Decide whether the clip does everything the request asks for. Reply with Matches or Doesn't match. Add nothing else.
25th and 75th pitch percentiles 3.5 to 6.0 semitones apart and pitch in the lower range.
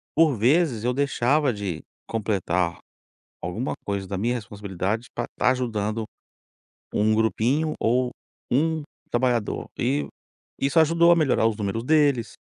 Matches